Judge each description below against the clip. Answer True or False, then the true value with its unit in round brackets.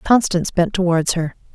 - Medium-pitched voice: True (175 Hz)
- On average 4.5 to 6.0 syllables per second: True (5.5 syllables/s)